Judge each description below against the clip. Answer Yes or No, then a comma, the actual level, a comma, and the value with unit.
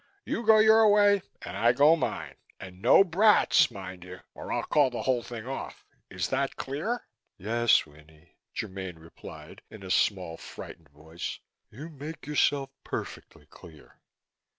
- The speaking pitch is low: Yes, low, 120 Hz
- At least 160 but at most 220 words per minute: No, average, 150 wpm